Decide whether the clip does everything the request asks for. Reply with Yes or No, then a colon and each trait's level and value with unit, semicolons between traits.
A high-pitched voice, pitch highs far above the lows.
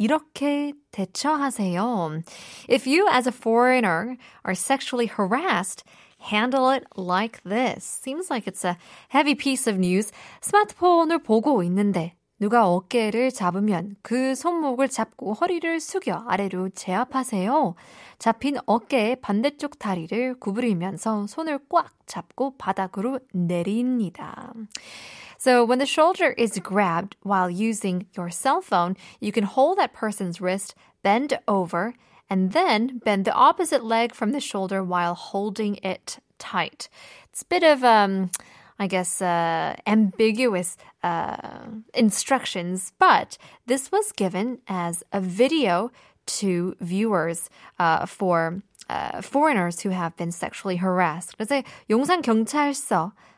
Yes: high, 220 Hz; wide, 5.7 semitones